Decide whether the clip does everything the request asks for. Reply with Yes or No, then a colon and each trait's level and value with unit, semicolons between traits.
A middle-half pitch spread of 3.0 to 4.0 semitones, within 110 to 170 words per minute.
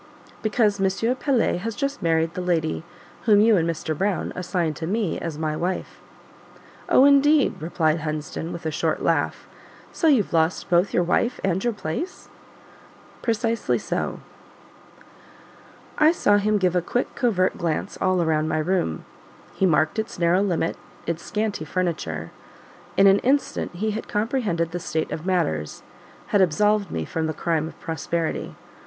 No: average, 4.7 semitones; average, 160 wpm